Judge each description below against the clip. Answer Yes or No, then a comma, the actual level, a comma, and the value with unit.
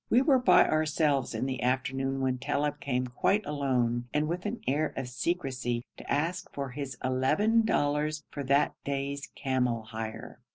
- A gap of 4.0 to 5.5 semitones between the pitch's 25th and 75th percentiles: No, average, 3.3 semitones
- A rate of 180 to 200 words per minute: No, average, 165 wpm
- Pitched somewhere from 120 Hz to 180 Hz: Yes, medium, 140 Hz